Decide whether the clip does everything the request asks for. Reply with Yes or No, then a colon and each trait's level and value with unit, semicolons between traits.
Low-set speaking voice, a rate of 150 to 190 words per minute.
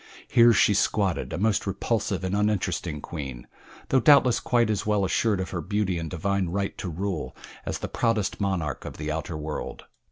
Yes: very low, 95 Hz; average, 185 wpm